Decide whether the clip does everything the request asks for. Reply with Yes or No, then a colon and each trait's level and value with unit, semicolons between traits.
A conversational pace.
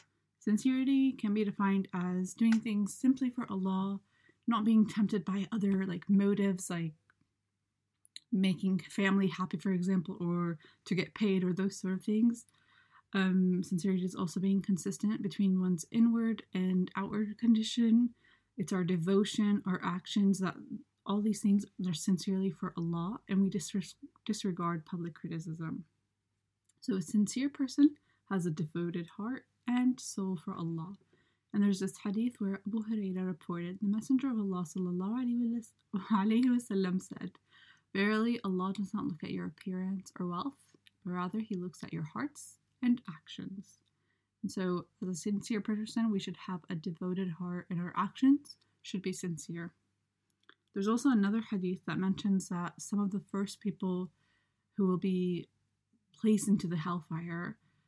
Yes: average, 150 wpm